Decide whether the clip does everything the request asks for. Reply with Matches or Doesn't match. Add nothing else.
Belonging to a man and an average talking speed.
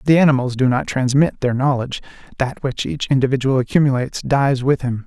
Matches